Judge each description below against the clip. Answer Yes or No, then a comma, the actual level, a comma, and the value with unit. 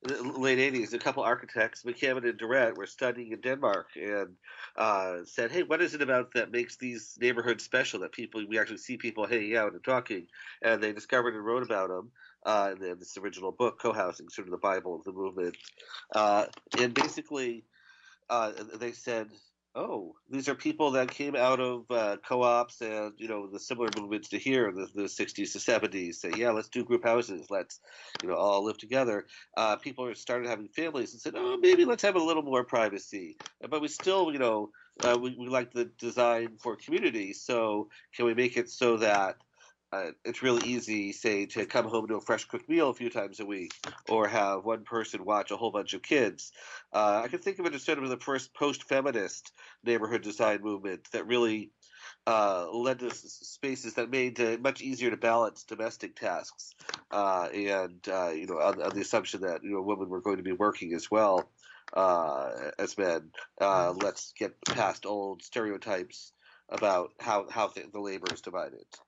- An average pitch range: Yes, average, 3.5 semitones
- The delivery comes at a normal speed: Yes, average, 195 wpm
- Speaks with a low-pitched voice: Yes, low, 120 Hz